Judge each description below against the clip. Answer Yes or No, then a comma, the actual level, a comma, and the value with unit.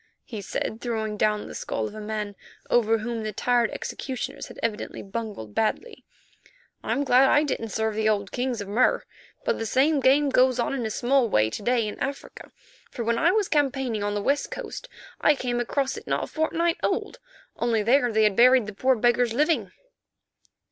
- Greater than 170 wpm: Yes, average, 195 wpm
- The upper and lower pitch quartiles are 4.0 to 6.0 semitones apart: No, average, 3.6 semitones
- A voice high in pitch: Yes, high, 235 Hz